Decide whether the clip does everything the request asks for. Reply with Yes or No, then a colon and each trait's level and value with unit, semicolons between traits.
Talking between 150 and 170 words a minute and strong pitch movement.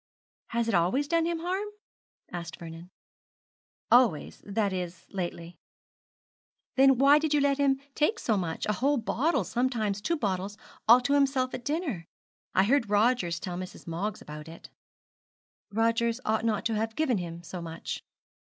Yes: average, 160 wpm; wide, 7.1 semitones